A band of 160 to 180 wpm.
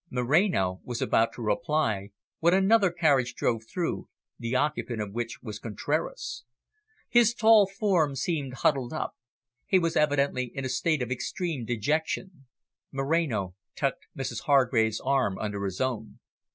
No: average, 140 wpm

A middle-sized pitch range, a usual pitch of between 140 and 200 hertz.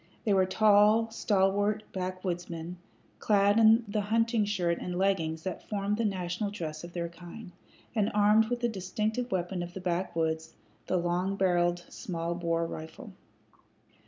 Yes: average, 3.3 semitones; high, 190 Hz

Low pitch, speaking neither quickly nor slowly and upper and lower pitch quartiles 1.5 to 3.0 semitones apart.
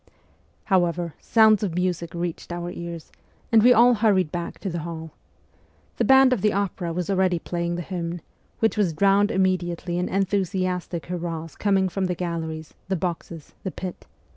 No: medium, 180 Hz; average, 165 wpm; narrow, 2.4 semitones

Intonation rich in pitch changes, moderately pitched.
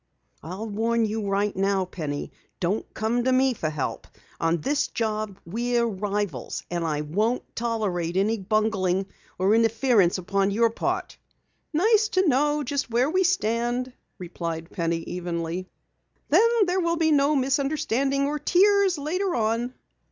No: wide, 6.9 semitones; high, 225 Hz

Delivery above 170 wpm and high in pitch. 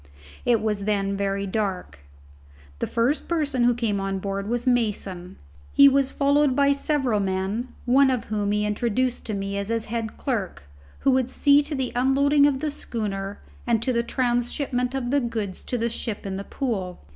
Yes: average, 185 wpm; high, 235 Hz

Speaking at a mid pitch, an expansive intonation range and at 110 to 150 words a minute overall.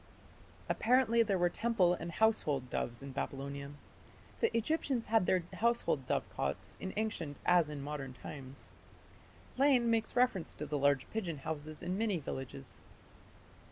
Yes: medium, 170 Hz; wide, 8.0 semitones; average, 140 wpm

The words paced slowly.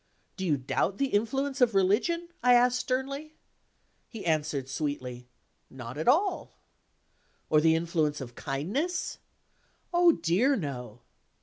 Yes: slow, 125 wpm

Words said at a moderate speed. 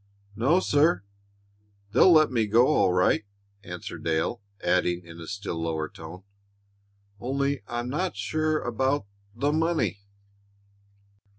No: slow, 130 wpm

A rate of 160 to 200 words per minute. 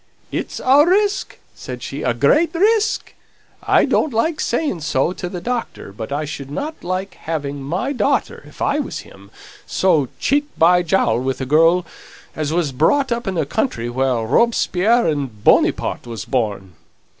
Yes: average, 165 wpm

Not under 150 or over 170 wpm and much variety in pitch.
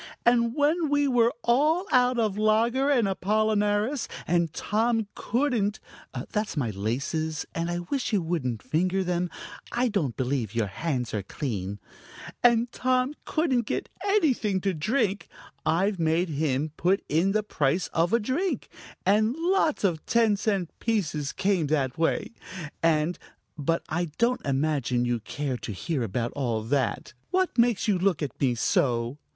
Yes: average, 155 wpm; wide, 8.2 semitones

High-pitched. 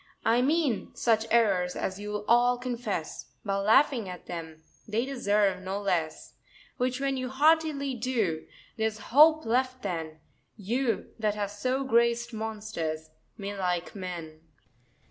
Yes: high, 220 Hz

